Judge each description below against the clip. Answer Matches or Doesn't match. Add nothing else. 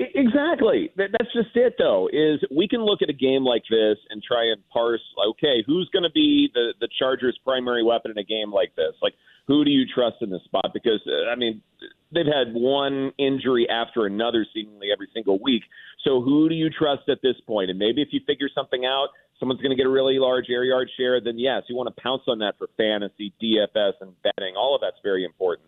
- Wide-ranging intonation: Matches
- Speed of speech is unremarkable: Doesn't match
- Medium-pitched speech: Doesn't match